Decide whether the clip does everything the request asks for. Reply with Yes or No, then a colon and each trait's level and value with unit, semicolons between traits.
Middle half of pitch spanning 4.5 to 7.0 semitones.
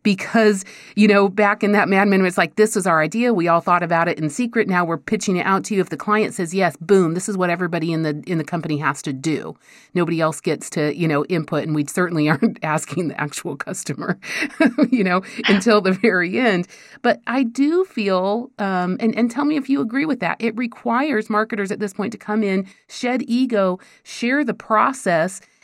Yes: average, 4.9 semitones